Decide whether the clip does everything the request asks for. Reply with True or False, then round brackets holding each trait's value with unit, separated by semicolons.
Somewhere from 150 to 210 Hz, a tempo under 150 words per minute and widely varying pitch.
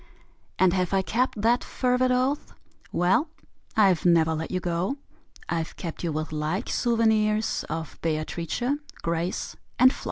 True (185 Hz; 140 wpm; 5.7 semitones)